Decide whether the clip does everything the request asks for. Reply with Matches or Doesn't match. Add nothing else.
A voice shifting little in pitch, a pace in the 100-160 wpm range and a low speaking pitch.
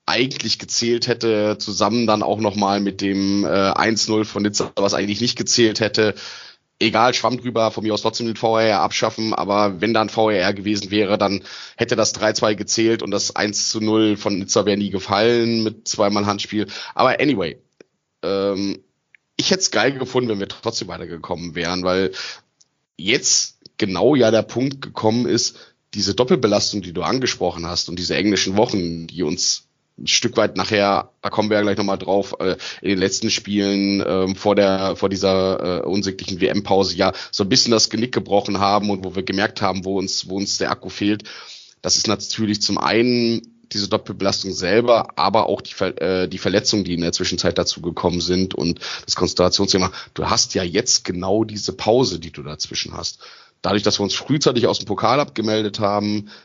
Doesn't match